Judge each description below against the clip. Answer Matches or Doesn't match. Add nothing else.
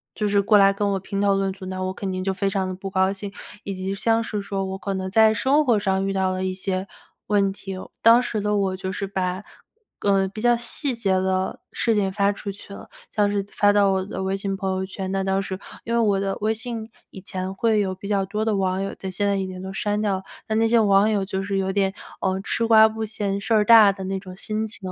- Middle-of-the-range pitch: Doesn't match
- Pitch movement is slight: Matches